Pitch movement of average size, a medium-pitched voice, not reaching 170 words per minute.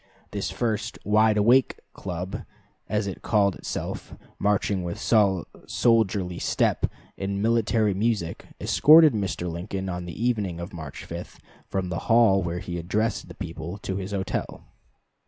No: average, 3.4 semitones; low, 100 Hz; average, 140 wpm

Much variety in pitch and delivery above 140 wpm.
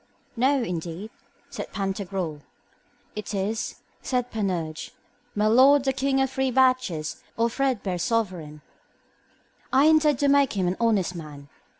No: wide, 6.6 semitones; slow, 135 wpm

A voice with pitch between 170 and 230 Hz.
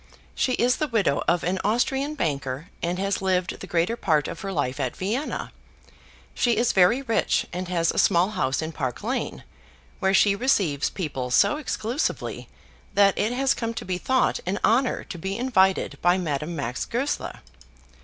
Yes: high, 190 Hz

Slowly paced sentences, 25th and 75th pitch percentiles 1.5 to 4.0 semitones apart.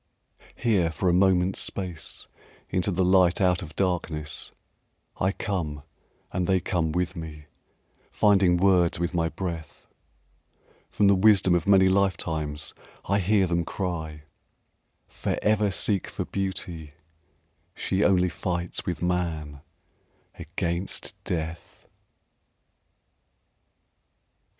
Yes: slow, 110 wpm; narrow, 2.6 semitones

